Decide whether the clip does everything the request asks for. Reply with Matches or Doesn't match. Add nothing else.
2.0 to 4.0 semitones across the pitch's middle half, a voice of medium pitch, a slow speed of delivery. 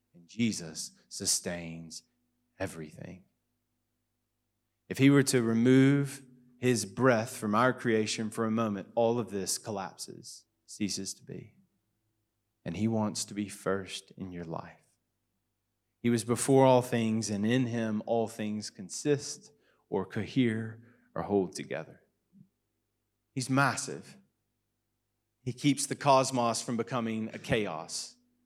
Doesn't match